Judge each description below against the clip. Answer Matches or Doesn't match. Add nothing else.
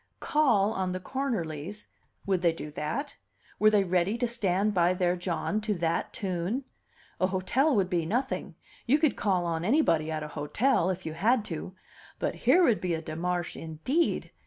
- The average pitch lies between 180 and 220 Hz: Matches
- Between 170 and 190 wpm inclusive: Matches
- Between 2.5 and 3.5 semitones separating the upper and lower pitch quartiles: Doesn't match